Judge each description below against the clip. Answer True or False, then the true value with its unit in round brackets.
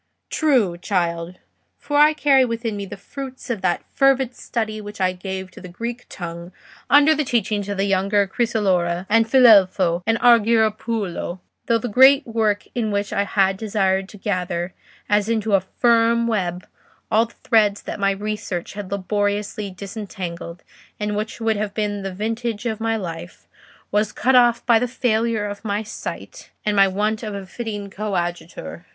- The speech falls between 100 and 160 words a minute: False (170 wpm)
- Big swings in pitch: False (3.2 semitones)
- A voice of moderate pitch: False (210 Hz)